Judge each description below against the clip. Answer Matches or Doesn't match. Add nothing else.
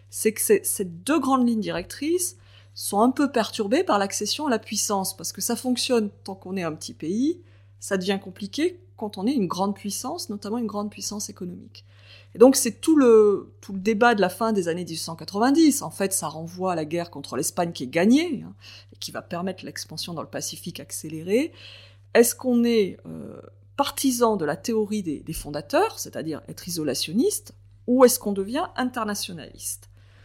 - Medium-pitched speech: Doesn't match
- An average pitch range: Doesn't match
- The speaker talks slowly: Doesn't match